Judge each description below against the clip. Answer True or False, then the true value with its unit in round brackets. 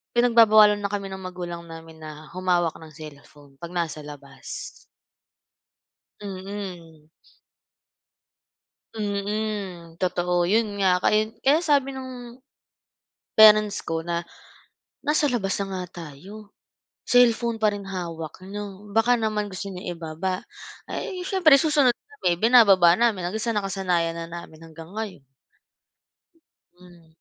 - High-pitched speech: True (195 Hz)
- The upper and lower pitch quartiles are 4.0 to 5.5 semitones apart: True (4.3 semitones)